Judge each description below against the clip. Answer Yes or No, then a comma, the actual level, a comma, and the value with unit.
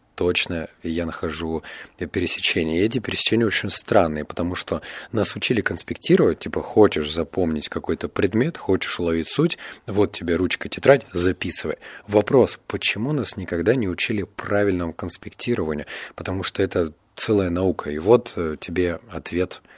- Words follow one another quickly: No, average, 135 wpm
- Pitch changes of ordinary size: No, narrow, 2.1 semitones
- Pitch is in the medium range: No, very low, 85 Hz